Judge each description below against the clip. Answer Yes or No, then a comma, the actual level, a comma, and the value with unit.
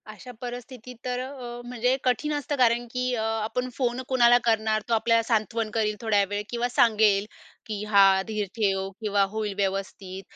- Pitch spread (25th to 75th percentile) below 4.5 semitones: Yes, average, 2.8 semitones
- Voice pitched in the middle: No, high, 225 Hz